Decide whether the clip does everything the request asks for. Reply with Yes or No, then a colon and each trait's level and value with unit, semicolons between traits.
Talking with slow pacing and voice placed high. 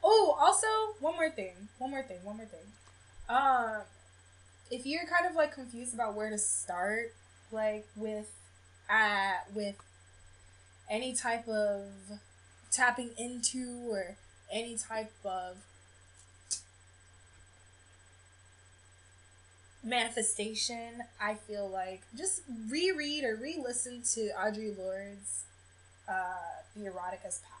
Yes: slow, 115 wpm; high, 210 Hz